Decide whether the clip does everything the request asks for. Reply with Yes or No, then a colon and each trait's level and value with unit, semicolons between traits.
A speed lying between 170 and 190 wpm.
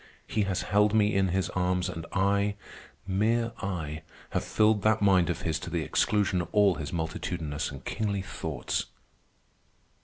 No: average, 160 wpm